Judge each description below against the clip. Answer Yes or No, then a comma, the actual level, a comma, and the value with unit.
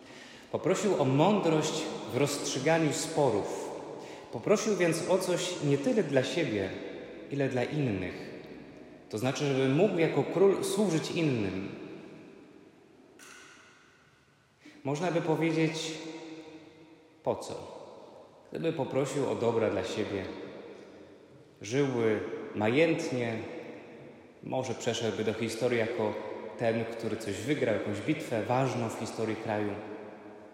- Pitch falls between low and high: Yes, medium, 145 Hz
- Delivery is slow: Yes, slow, 105 wpm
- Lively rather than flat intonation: Yes, wide, 6.2 semitones